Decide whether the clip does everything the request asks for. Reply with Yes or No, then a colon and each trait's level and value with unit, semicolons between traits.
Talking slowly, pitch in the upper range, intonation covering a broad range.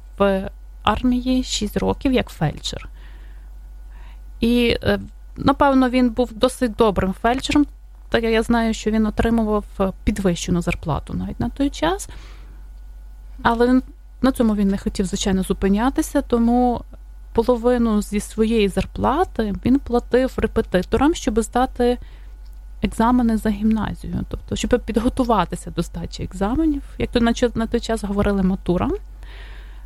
No: slow, 120 wpm; high, 225 Hz; average, 4.1 semitones